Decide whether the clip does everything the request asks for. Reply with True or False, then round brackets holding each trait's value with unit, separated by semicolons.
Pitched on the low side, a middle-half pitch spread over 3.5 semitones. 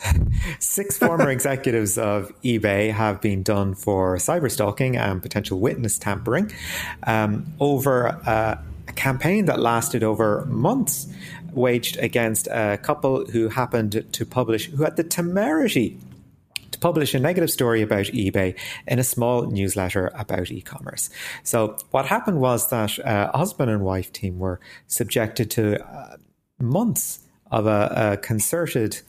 True (115 Hz; 4.4 semitones)